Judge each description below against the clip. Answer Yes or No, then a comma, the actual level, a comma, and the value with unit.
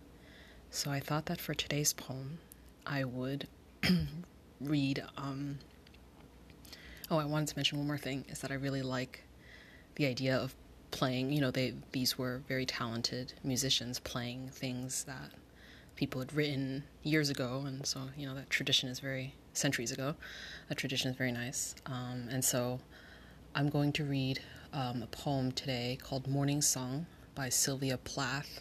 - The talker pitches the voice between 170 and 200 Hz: No, low, 135 Hz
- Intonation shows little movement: Yes, narrow, 2.0 semitones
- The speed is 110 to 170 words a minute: Yes, average, 160 wpm